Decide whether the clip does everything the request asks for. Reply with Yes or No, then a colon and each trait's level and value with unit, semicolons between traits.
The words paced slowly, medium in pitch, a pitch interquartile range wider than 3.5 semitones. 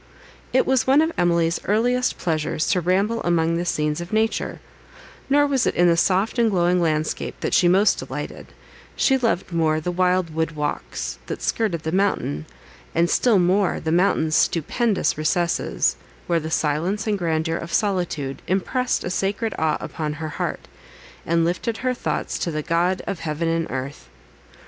No: average, 170 wpm; medium, 175 Hz; average, 4.1 semitones